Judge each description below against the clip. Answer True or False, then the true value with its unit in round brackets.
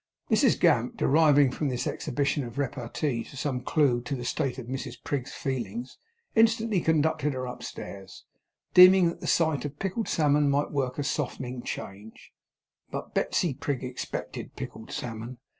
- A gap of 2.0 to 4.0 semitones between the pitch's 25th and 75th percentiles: True (3.3 semitones)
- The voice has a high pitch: False (135 Hz)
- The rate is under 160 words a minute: True (150 wpm)